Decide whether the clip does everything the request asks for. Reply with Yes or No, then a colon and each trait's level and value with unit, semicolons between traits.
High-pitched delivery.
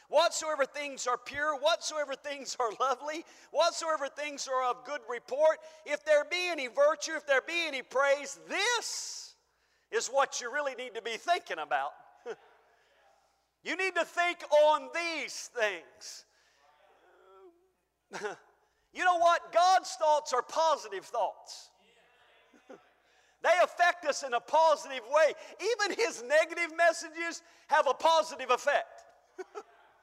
Yes: very high, 315 Hz